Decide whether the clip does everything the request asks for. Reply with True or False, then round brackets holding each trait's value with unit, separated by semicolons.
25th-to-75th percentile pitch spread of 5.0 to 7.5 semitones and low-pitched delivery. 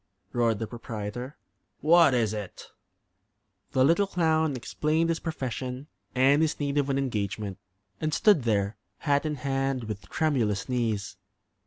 True (5.5 semitones; 130 Hz)